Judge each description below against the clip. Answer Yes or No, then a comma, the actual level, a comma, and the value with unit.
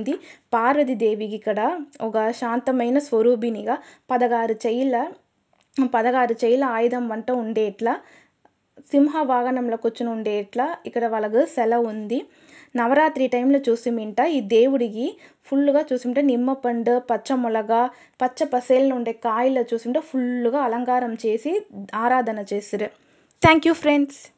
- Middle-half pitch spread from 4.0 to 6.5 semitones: No, average, 2.8 semitones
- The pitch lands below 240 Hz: No, high, 245 Hz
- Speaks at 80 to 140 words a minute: Yes, average, 110 wpm